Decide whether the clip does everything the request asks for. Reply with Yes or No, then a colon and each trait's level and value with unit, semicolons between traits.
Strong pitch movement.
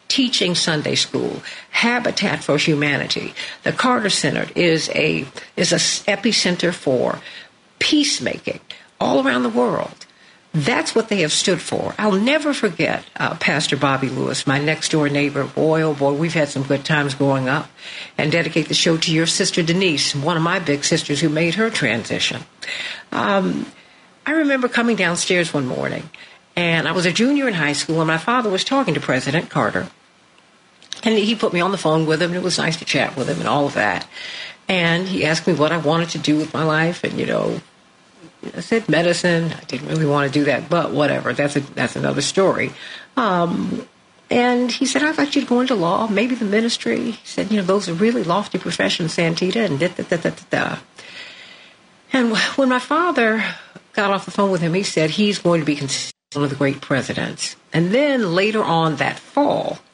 Yes: wide, 6.4 semitones